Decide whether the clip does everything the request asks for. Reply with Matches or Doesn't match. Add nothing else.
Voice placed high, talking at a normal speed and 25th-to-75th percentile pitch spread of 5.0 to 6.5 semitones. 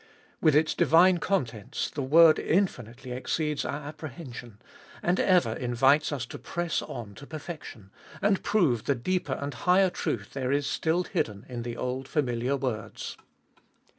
Doesn't match